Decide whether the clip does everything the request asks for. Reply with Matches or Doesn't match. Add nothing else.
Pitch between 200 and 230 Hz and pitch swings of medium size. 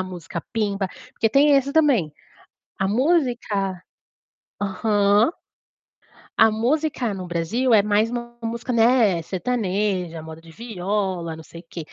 Matches